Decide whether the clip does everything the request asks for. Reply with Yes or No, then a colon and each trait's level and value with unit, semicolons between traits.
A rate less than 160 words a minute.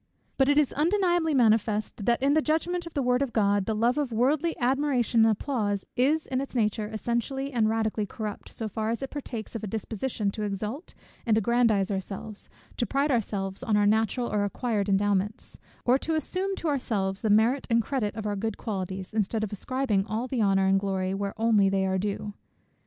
No: average, 200 wpm